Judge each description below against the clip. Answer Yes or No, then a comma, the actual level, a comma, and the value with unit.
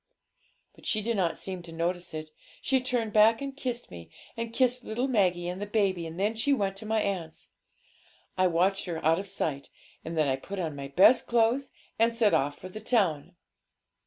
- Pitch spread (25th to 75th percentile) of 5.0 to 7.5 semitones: Yes, average, 5.3 semitones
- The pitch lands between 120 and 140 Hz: No, high, 195 Hz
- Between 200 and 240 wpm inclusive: Yes, fast, 205 wpm